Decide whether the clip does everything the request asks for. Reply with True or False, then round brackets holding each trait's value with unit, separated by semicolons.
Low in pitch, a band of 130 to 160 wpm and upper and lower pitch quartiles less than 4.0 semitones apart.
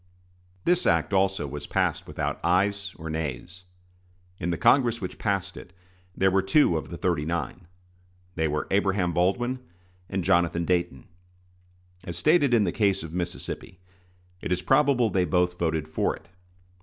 True (90 Hz; 155 wpm; 2.9 semitones)